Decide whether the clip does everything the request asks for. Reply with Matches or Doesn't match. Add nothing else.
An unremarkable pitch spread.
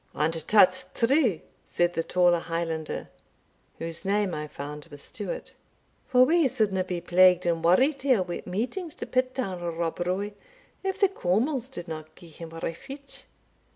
Doesn't match